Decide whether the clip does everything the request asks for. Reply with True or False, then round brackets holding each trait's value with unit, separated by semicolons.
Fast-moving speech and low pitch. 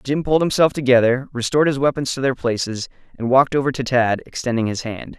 True (210 wpm; 130 Hz)